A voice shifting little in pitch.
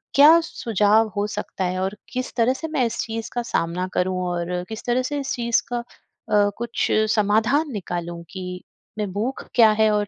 No: average, 4.5 semitones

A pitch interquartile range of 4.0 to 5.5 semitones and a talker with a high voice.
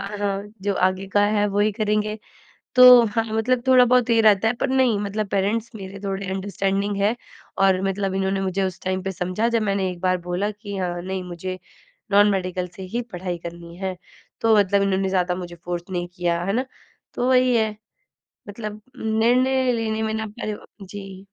No: average, 2.7 semitones; high, 200 Hz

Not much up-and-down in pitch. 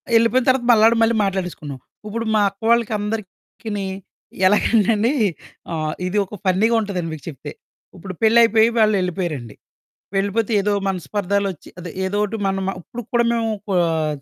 No: average, 3.6 semitones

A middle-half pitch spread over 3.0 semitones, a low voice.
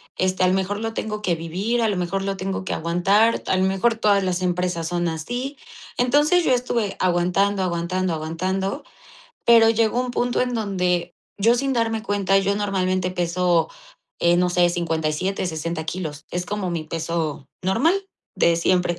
No: average, 3.6 semitones; medium, 185 Hz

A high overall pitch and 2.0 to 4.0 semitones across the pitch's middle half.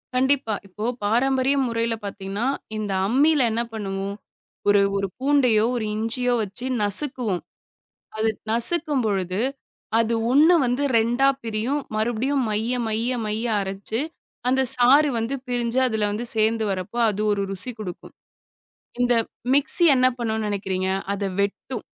Yes: high, 225 Hz; average, 3.6 semitones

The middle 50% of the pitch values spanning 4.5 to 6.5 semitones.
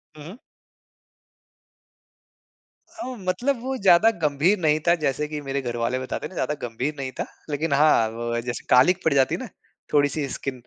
Yes: average, 5.1 semitones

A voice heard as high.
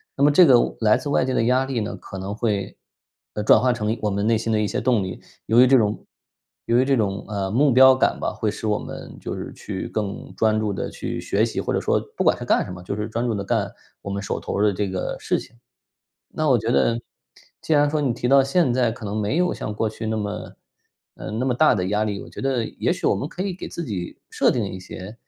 No: low, 110 Hz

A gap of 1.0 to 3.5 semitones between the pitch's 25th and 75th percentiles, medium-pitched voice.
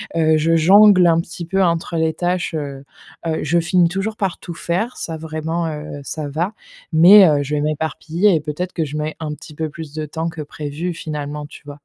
Yes: narrow, 2.5 semitones; medium, 160 Hz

